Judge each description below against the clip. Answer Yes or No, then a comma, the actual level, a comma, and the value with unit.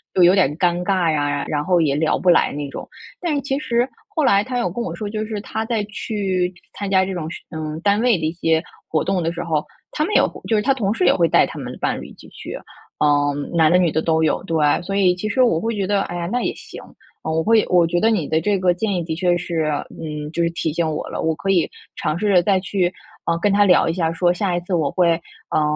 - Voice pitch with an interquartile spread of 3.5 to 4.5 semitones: Yes, average, 4.0 semitones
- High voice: No, medium, 180 Hz